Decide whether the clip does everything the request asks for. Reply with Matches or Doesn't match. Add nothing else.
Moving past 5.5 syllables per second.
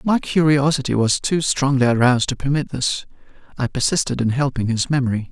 Matches